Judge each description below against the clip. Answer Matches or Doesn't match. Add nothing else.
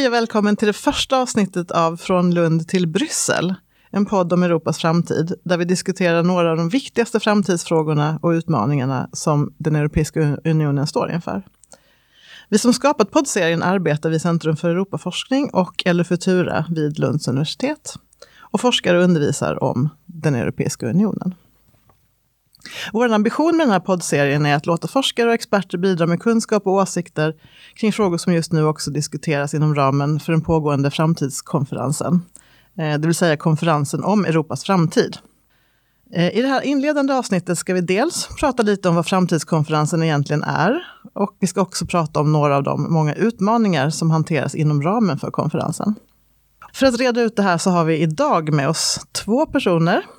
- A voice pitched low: Doesn't match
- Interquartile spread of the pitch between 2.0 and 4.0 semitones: Doesn't match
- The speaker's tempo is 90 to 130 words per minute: Doesn't match